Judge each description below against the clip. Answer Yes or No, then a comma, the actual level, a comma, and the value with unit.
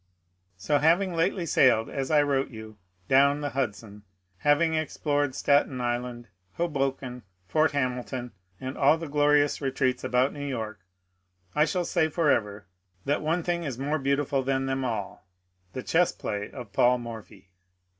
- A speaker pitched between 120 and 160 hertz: Yes, low, 135 Hz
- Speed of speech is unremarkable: Yes, average, 155 wpm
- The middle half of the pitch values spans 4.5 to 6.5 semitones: No, average, 3.5 semitones